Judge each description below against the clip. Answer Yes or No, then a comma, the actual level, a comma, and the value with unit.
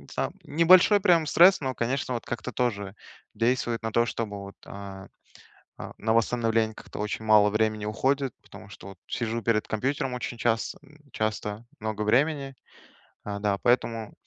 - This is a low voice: Yes, low, 115 Hz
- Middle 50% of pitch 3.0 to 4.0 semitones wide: Yes, average, 3.5 semitones